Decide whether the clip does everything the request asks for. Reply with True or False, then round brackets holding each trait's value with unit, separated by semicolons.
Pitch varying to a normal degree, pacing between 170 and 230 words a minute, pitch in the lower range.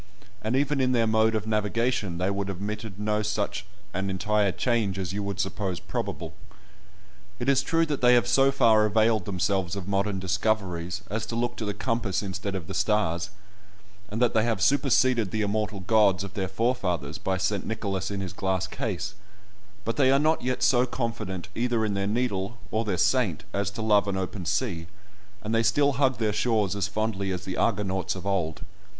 True (3.2 semitones; 195 wpm; 105 Hz)